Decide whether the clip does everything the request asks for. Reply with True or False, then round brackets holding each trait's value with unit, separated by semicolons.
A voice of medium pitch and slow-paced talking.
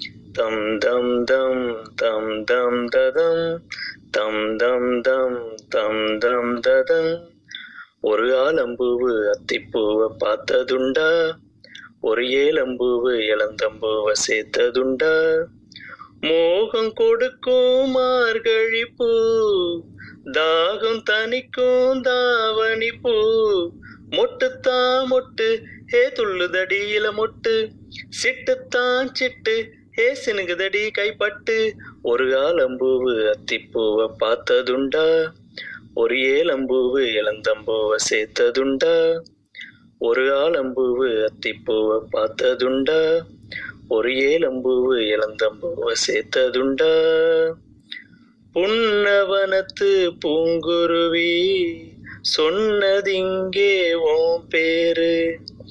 False (255 Hz; 60 wpm)